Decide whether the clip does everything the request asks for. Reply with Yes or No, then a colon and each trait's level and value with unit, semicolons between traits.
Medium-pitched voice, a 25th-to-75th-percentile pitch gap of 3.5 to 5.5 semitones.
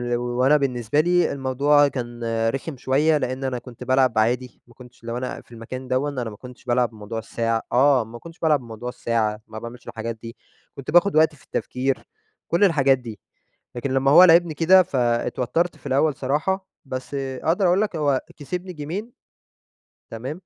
No: low, 130 Hz; average, 4.0 semitones